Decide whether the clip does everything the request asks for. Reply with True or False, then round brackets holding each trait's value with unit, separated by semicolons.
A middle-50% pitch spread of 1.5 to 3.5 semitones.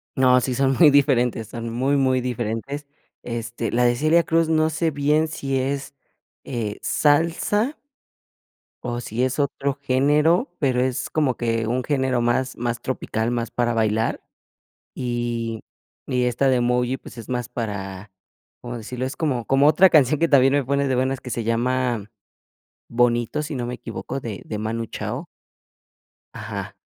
True (2.9 semitones)